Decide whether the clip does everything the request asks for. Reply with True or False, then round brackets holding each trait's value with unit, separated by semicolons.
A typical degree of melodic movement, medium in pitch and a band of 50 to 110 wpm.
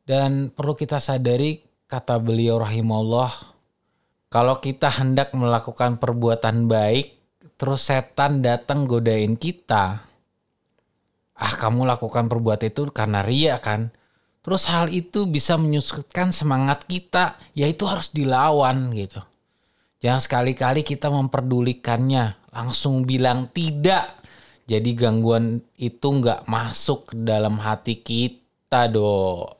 False (3.8 semitones; 125 Hz; 105 wpm)